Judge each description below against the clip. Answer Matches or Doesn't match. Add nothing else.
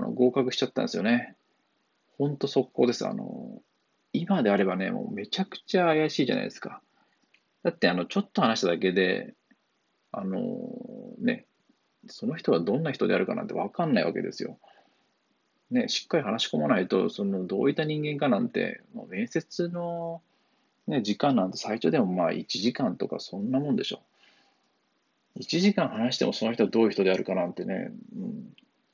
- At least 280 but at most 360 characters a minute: Matches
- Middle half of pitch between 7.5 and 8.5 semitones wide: Matches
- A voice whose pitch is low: Doesn't match